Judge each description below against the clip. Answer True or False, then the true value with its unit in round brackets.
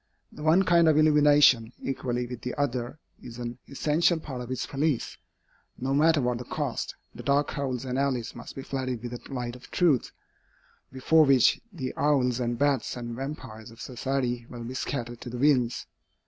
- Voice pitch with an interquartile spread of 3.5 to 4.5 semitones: False (3.1 semitones)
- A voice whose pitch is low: True (130 Hz)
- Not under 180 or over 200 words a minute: True (185 wpm)